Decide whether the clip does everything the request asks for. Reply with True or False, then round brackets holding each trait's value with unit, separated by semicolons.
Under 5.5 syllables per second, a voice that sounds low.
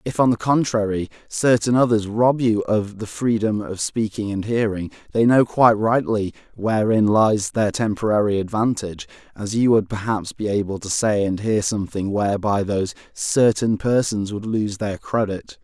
True (4.8 syllables/s; 105 Hz)